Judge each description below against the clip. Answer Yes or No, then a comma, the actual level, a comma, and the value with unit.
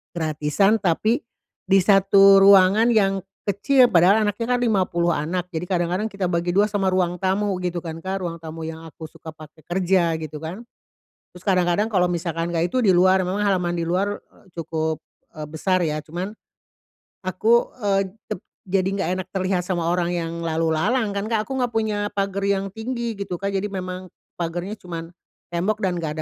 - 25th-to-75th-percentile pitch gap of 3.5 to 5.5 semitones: No, average, 2.9 semitones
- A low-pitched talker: No, medium, 185 Hz